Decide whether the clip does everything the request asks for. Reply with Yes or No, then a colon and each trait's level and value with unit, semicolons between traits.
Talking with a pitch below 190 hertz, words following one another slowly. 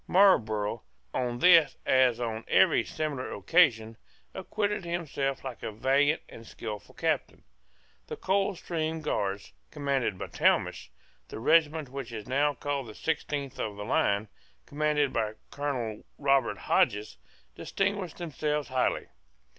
Yes: low, 135 Hz; slow, 130 wpm